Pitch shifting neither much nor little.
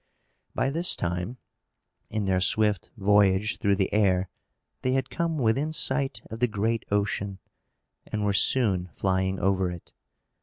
Yes: average, 3.4 semitones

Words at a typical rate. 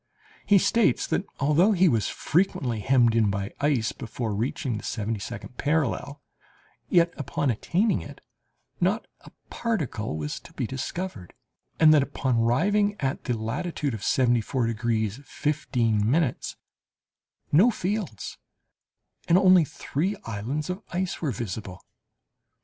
No: slow, 130 wpm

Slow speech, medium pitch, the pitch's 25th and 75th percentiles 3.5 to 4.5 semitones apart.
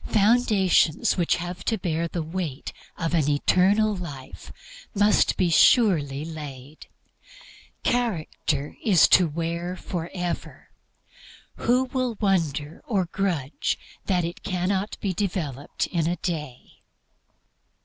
Yes: slow, 110 wpm; medium, 175 Hz; average, 3.9 semitones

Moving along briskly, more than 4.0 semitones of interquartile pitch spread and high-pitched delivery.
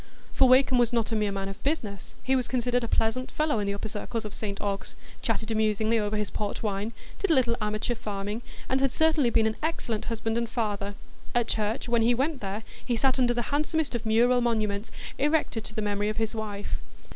No: fast, 215 wpm; average, 2.9 semitones; high, 225 Hz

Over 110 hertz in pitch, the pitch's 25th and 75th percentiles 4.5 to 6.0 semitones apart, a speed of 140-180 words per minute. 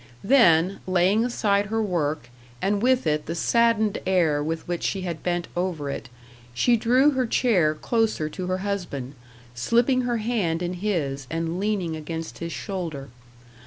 Yes: medium, 185 Hz; average, 5.2 semitones; average, 160 wpm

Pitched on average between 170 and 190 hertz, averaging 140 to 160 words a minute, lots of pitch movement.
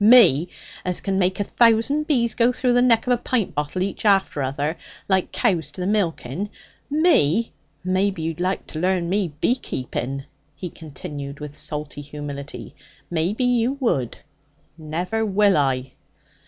Yes: medium, 185 Hz; average, 155 wpm; wide, 7.0 semitones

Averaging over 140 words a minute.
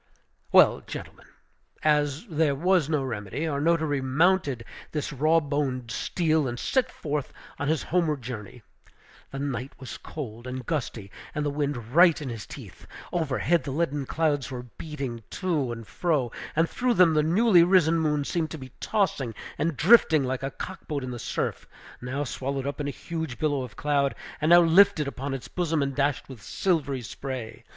Yes: average, 180 wpm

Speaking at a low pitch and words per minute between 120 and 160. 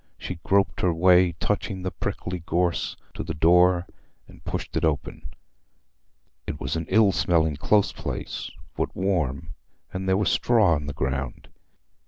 Yes: very low, 90 Hz; average, 155 wpm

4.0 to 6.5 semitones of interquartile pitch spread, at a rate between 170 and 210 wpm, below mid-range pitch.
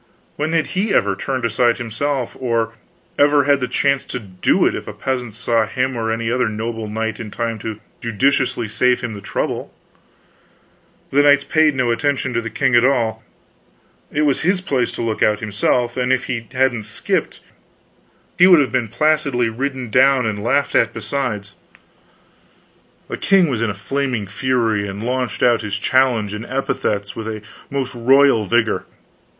No: average, 3.5 semitones; average, 175 wpm; low, 120 Hz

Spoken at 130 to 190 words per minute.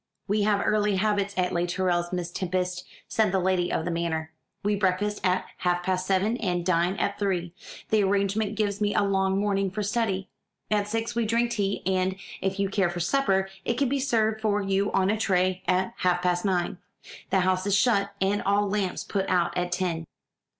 No: average, 200 wpm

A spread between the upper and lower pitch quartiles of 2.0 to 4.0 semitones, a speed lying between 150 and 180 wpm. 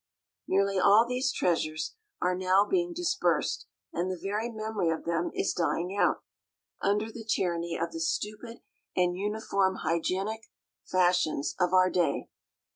No: average, 3.7 semitones; average, 140 wpm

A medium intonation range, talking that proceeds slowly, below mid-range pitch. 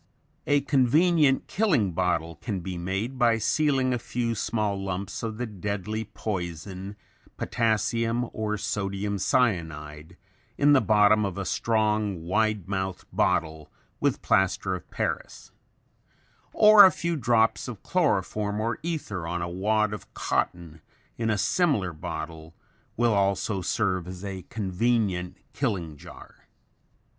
Yes: average, 4.1 semitones; slow, 130 wpm; low, 105 Hz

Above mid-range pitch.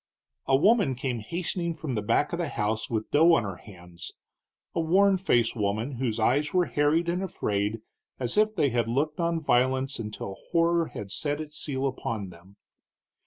No: low, 135 Hz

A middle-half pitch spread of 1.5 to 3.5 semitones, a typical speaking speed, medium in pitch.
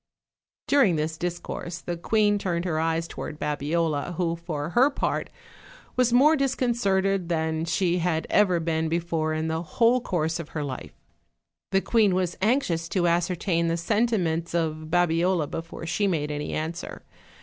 Yes: average, 3.1 semitones; average, 160 wpm; medium, 170 Hz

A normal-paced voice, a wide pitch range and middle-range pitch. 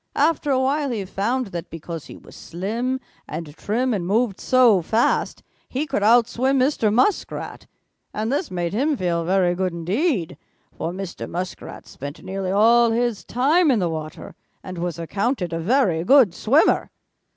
No: average, 165 wpm; wide, 6.5 semitones; high, 210 Hz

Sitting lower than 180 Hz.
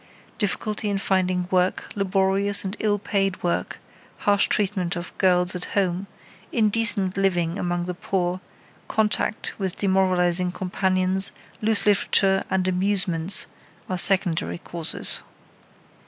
No: high, 190 Hz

